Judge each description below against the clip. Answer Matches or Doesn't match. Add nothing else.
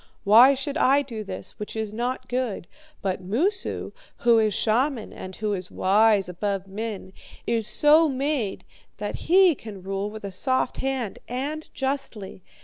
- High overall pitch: Matches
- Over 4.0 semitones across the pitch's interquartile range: Matches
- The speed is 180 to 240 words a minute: Doesn't match